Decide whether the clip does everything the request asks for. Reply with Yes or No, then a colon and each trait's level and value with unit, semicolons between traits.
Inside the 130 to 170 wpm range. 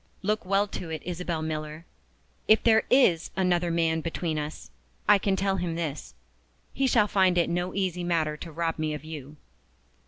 No: average, 180 wpm